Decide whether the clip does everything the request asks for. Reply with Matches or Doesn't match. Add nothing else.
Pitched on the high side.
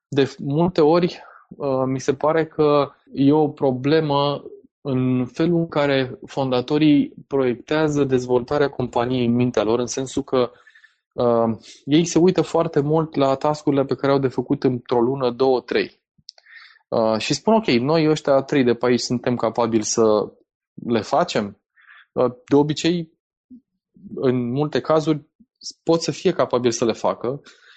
Doesn't match